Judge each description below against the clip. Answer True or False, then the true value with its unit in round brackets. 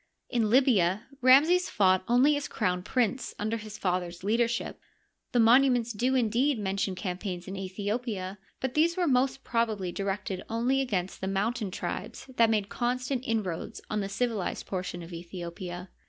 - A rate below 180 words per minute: True (155 wpm)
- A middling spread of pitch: True (4.8 semitones)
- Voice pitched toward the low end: False (215 Hz)